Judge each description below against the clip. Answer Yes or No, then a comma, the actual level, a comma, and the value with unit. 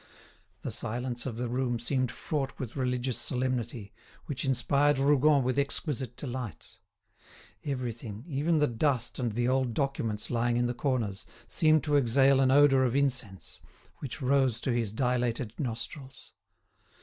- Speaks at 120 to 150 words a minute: Yes, average, 145 wpm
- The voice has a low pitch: Yes, low, 130 Hz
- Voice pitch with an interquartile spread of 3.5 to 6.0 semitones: No, narrow, 2.5 semitones